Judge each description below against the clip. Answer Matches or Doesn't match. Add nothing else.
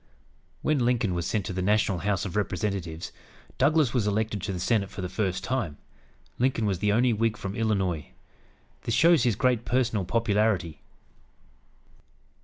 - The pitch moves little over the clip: Doesn't match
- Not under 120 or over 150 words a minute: Doesn't match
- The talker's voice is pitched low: Matches